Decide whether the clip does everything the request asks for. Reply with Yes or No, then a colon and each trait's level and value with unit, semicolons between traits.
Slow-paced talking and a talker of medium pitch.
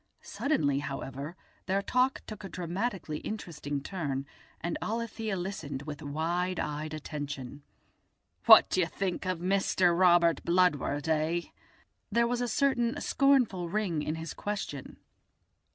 Yes: slow, 130 wpm; medium, 175 Hz